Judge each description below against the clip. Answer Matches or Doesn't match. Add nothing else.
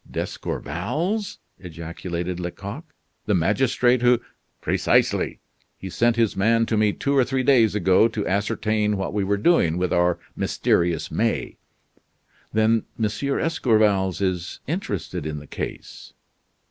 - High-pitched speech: Doesn't match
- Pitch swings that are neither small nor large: Matches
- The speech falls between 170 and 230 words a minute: Doesn't match